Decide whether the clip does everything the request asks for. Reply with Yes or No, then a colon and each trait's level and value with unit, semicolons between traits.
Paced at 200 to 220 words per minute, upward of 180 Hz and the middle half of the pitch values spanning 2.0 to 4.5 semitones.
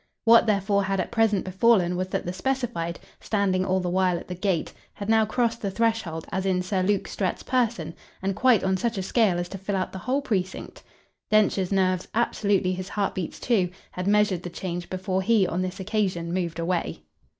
Yes: fast, 205 wpm; high, 190 Hz; average, 2.8 semitones